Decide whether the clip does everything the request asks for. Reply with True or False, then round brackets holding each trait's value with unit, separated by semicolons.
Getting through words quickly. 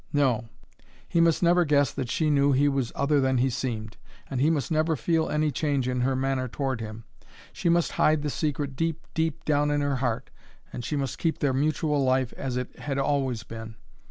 True (210 wpm)